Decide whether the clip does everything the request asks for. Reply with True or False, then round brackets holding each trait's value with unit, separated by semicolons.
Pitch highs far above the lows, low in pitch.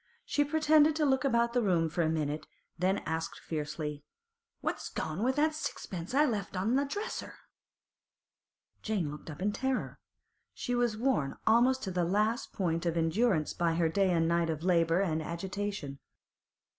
False (6.9 semitones; 190 Hz)